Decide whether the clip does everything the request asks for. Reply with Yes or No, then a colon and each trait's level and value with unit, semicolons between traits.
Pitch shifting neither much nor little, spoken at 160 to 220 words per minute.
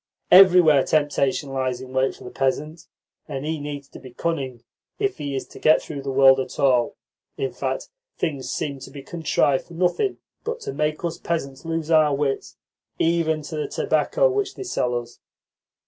Yes: average, 3.8 semitones; average, 185 wpm